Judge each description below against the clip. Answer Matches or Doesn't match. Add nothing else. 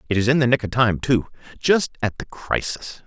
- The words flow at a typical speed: Doesn't match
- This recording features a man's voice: Matches